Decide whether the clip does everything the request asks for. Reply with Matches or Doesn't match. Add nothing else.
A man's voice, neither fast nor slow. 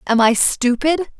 Doesn't match